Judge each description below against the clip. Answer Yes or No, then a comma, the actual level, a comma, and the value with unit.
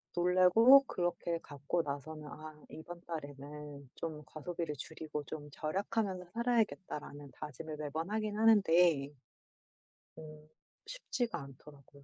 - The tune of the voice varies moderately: Yes, average, 3.5 semitones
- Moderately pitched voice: Yes, medium, 160 Hz